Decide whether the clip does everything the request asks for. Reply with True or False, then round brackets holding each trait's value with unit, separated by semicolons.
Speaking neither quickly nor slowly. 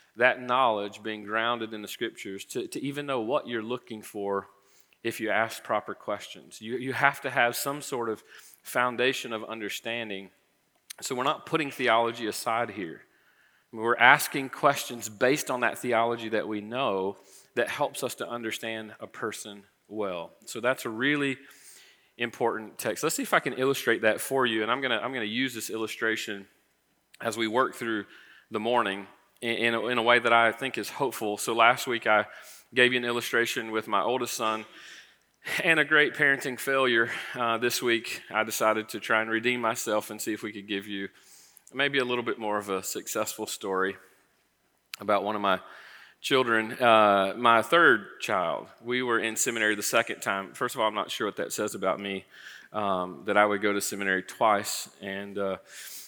True (190 wpm)